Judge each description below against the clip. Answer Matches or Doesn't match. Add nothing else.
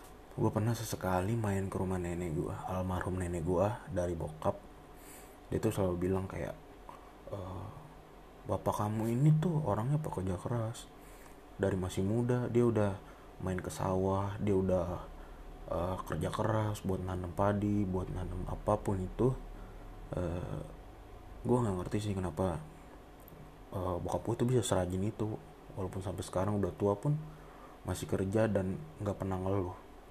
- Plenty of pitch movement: Doesn't match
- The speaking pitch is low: Matches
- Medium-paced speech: Doesn't match